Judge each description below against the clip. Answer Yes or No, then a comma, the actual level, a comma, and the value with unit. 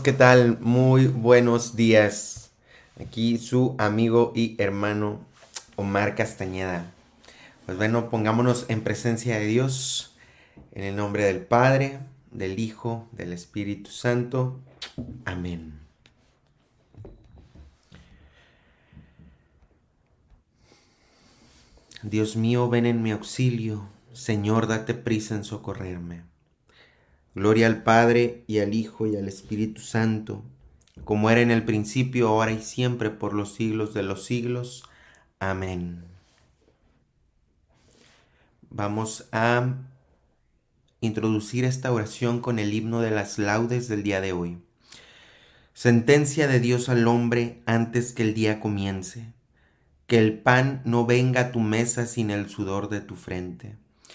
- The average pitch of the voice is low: Yes, low, 110 Hz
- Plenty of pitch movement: No, average, 3.1 semitones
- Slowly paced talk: Yes, slow, 115 wpm